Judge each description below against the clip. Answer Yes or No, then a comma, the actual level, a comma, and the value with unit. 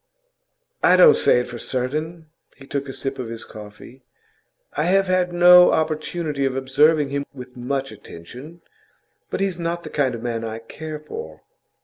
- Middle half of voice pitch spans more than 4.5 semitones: Yes, average, 5.1 semitones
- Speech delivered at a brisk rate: No, average, 170 wpm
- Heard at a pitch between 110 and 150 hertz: Yes, medium, 140 Hz